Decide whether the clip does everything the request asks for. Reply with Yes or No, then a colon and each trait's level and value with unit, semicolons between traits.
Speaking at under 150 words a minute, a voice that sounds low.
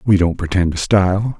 No: fast, 215 wpm; very low, 95 Hz